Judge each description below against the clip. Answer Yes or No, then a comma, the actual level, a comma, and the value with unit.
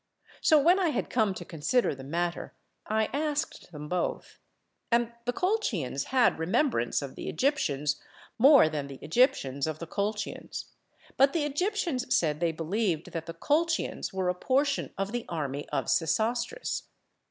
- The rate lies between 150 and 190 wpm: Yes, average, 155 wpm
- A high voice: Yes, high, 210 Hz